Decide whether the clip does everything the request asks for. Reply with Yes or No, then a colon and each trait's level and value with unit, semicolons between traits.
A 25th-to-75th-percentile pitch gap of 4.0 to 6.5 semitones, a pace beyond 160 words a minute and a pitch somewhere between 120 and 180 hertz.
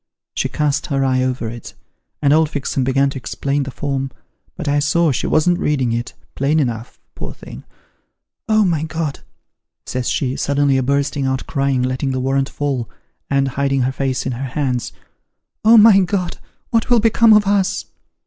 No: average, 3.1 semitones; average, 185 wpm; medium, 140 Hz